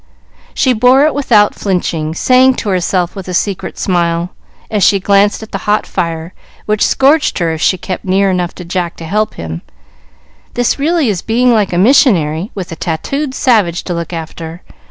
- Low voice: No, high, 190 Hz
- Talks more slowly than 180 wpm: No, average, 185 wpm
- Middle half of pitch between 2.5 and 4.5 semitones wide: No, average, 4.9 semitones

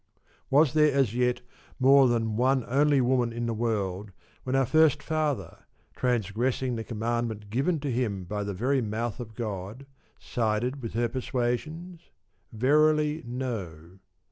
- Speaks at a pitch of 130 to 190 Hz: No, low, 120 Hz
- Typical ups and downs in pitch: Yes, average, 3.8 semitones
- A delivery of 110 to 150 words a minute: Yes, average, 140 wpm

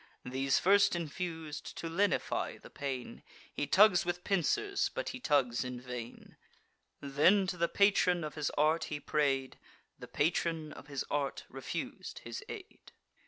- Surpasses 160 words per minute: No, average, 150 wpm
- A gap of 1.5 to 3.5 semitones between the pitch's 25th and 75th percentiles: No, average, 4.5 semitones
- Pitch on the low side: No, medium, 155 Hz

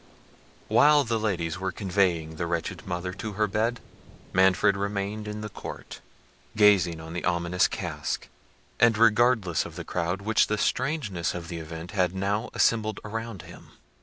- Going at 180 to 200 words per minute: No, average, 160 wpm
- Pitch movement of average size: Yes, average, 3.6 semitones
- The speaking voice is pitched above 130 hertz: No, low, 100 Hz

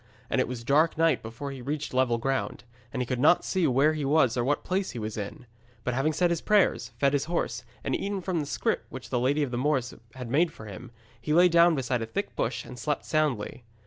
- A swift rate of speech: Yes, fast, 250 wpm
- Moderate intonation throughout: Yes, average, 4.3 semitones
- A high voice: No, low, 135 Hz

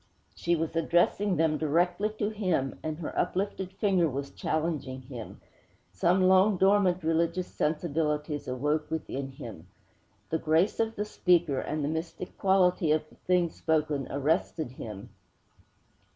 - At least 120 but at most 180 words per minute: Yes, average, 140 wpm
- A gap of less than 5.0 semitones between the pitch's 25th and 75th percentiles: Yes, average, 3.5 semitones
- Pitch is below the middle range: No, medium, 160 Hz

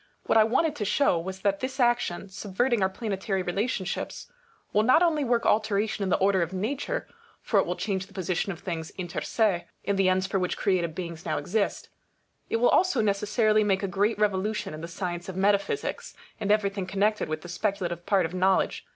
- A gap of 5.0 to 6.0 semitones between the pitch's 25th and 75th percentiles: No, average, 2.7 semitones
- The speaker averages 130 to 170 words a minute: No, fast, 205 wpm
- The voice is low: No, high, 195 Hz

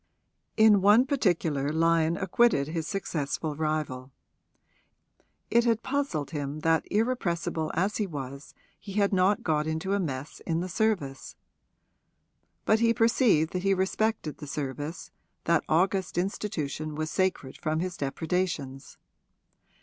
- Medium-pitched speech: Yes, medium, 170 Hz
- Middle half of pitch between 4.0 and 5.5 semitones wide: Yes, average, 4.8 semitones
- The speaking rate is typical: No, slow, 130 wpm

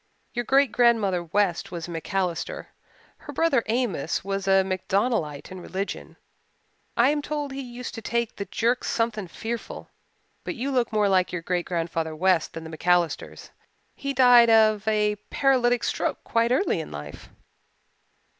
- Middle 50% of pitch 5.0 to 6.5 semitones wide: Yes, average, 5.3 semitones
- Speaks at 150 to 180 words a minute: Yes, average, 155 wpm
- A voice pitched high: Yes, high, 210 Hz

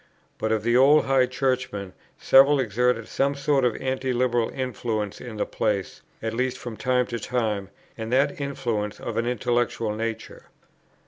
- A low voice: Yes, low, 120 Hz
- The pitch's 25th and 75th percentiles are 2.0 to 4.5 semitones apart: Yes, average, 2.8 semitones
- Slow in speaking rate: No, average, 165 wpm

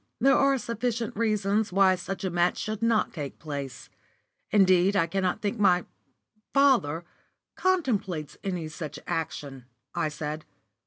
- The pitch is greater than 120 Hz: Yes, high, 190 Hz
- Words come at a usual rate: No, slow, 130 wpm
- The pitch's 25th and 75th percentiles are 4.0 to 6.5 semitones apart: Yes, wide, 5.4 semitones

